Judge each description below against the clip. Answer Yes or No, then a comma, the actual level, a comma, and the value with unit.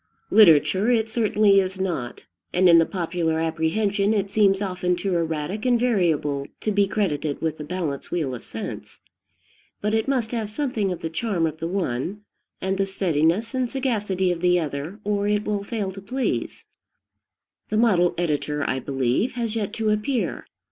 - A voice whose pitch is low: No, high, 190 Hz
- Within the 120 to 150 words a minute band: No, average, 175 wpm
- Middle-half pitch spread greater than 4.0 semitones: Yes, average, 4.6 semitones